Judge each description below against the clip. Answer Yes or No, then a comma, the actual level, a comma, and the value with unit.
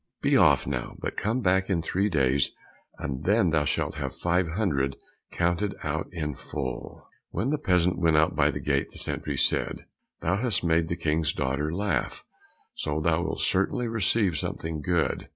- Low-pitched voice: Yes, very low, 85 Hz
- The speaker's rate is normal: Yes, average, 175 wpm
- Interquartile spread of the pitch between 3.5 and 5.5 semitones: Yes, average, 4.2 semitones